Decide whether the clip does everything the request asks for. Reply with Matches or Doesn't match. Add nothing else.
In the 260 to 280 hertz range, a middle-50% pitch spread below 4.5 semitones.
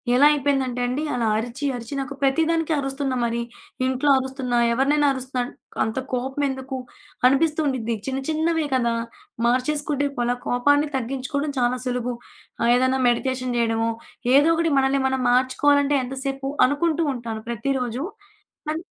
Matches